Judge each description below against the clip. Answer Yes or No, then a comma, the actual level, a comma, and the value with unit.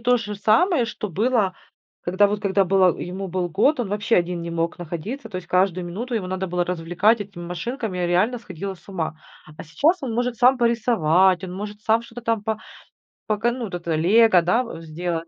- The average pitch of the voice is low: No, high, 195 Hz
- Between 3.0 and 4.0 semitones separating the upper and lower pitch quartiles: No, average, 4.5 semitones